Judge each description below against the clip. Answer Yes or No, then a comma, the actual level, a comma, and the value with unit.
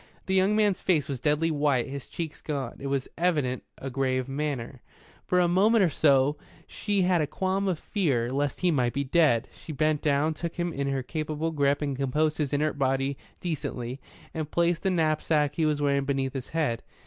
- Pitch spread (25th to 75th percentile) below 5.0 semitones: Yes, average, 3.3 semitones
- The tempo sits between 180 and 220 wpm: Yes, average, 200 wpm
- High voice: No, medium, 150 Hz